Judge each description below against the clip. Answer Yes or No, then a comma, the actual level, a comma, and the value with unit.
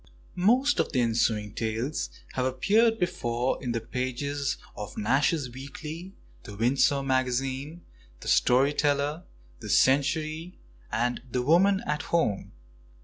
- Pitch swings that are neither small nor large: Yes, average, 4.2 semitones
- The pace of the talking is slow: Yes, slow, 125 wpm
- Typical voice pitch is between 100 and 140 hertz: Yes, low, 135 Hz